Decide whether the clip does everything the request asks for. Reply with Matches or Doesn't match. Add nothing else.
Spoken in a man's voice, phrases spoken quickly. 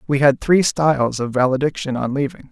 Doesn't match